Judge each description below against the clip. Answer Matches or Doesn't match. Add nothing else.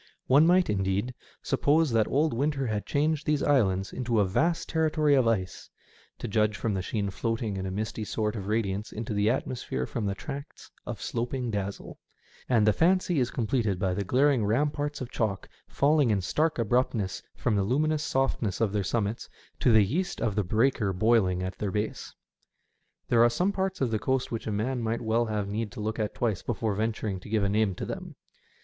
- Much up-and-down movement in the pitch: Doesn't match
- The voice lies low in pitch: Matches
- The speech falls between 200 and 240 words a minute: Matches